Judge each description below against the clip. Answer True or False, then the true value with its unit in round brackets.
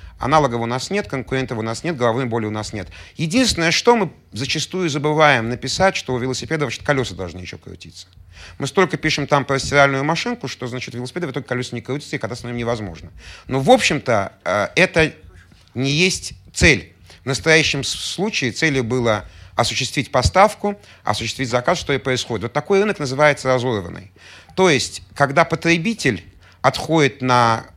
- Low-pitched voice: True (130 Hz)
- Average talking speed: False (165 wpm)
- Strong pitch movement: True (6.7 semitones)